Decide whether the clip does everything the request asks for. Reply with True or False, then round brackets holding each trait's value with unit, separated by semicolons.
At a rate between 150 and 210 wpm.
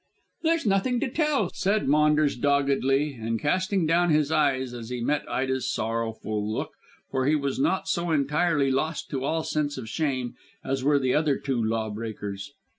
True (175 wpm)